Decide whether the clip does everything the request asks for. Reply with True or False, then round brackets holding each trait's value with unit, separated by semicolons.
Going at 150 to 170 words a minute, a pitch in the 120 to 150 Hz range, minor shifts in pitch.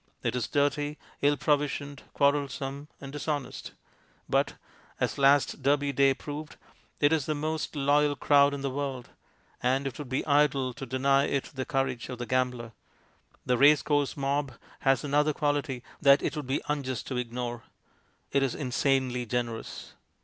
True (160 wpm; 140 Hz; 1.9 semitones)